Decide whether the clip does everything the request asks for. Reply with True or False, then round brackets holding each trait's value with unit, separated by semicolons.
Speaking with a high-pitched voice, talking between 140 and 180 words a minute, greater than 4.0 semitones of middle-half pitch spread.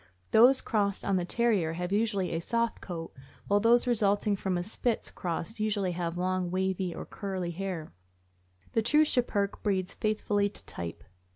False (200 Hz; 165 wpm; 3.4 semitones)